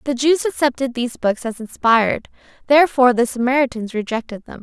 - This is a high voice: Yes, very high, 250 Hz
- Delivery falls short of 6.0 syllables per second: No, 6.1 syllables/s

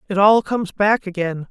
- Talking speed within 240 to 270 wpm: No, average, 200 wpm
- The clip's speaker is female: Yes, female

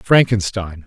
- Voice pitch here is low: Yes, low, 100 Hz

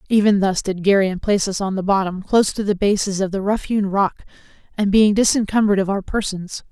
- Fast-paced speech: Yes, fast, 215 wpm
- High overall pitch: Yes, high, 200 Hz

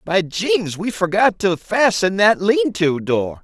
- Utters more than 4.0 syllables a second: No, 3.6 syllables/s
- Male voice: Yes, male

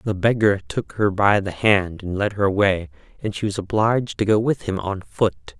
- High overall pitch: No, low, 100 Hz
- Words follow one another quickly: Yes, fast, 225 wpm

